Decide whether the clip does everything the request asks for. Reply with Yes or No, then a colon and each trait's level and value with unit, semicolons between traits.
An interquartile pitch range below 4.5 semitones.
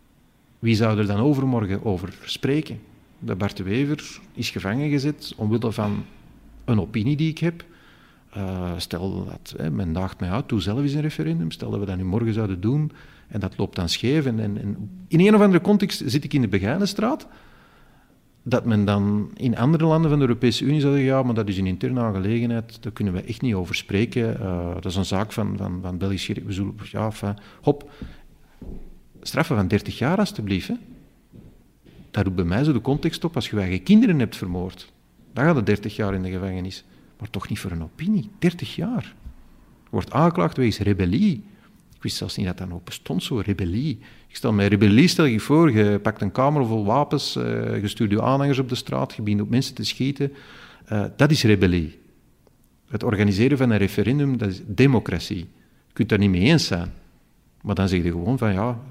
No: wide, 5.6 semitones